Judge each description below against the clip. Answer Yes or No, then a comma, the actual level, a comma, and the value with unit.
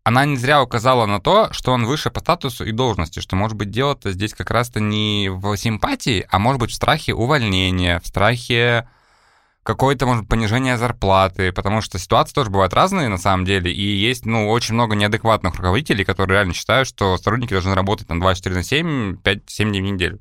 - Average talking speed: No, fast, 195 wpm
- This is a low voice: Yes, low, 110 Hz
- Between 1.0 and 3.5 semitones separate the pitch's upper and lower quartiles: No, average, 4.3 semitones